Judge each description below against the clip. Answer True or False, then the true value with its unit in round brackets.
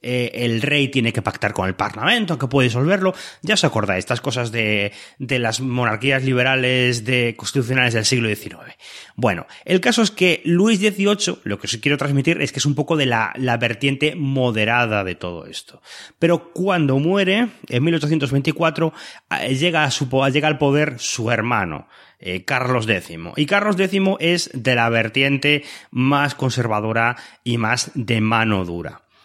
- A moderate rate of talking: True (165 wpm)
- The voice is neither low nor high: False (130 Hz)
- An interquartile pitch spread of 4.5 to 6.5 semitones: True (4.9 semitones)